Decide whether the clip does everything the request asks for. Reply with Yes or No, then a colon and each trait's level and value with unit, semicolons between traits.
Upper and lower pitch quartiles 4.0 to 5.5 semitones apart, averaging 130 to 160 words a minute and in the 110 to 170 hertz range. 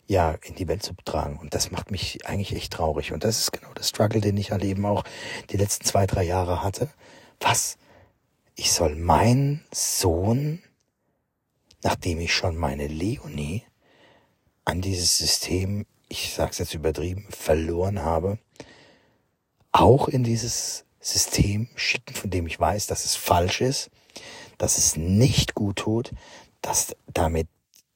No: average, 4.7 semitones; average, 150 wpm; very low, 95 Hz